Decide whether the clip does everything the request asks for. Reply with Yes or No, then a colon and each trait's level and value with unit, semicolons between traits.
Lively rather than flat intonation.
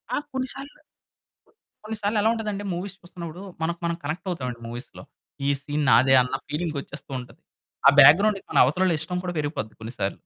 Yes: wide, 6.0 semitones